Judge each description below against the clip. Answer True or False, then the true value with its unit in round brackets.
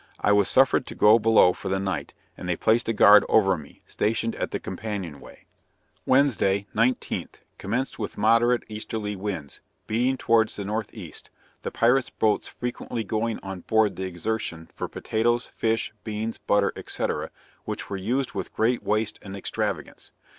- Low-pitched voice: True (110 Hz)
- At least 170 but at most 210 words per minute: False (160 wpm)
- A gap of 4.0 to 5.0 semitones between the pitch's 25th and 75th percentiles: False (2.7 semitones)